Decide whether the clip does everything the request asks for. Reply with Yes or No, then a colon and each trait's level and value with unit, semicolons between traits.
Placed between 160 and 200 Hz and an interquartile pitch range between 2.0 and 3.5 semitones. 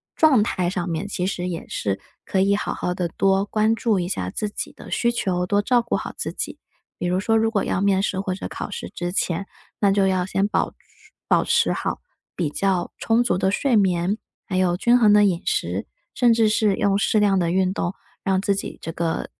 Yes: high, 195 Hz; narrow, 2.6 semitones